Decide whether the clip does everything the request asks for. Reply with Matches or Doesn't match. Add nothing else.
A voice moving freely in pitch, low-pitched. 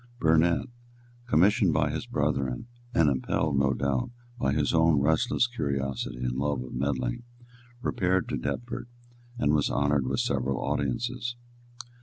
Doesn't match